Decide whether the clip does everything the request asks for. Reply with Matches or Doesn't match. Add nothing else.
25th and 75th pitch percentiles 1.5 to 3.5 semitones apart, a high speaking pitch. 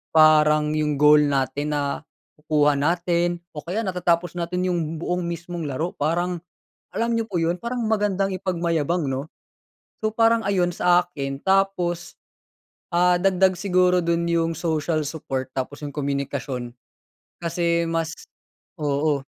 Doesn't match